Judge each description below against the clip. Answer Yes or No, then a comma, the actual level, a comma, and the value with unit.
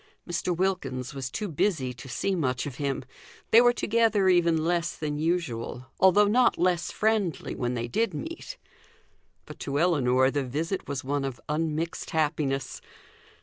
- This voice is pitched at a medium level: Yes, medium, 160 Hz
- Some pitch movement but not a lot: No, wide, 5.7 semitones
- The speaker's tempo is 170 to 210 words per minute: No, average, 155 wpm